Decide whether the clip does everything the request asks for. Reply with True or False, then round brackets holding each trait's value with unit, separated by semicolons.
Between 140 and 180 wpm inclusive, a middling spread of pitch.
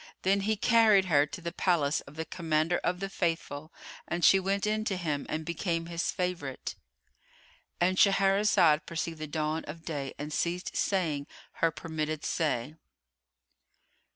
True (150 wpm; 3.5 semitones)